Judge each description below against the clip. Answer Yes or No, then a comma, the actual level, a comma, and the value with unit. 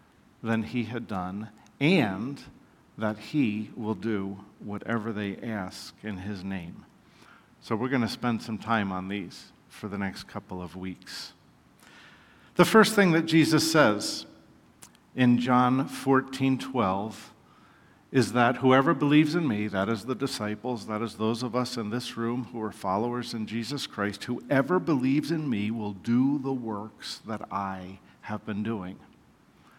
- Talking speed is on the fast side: No, average, 155 wpm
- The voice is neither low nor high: No, low, 115 Hz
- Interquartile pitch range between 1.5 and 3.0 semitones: No, average, 3.7 semitones